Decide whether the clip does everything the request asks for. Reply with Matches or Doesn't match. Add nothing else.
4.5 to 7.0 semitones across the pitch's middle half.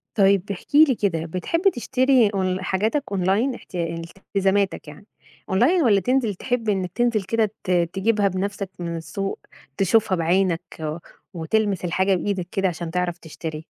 Doesn't match